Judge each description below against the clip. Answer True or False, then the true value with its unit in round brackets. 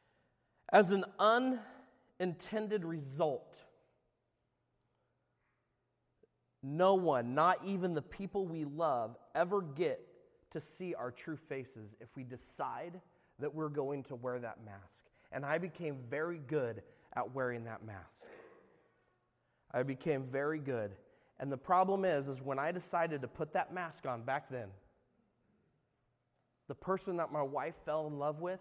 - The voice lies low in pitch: False (150 Hz)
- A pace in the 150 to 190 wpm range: False (140 wpm)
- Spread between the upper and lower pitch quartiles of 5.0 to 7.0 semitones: True (5.6 semitones)